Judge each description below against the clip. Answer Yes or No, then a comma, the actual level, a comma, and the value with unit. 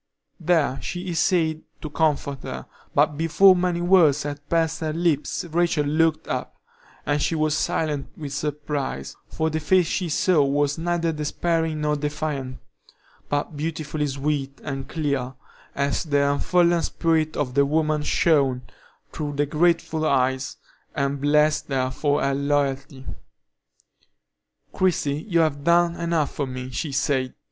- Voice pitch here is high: No, medium, 150 Hz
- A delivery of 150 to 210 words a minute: No, average, 140 wpm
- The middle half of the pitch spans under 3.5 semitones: Yes, narrow, 2.5 semitones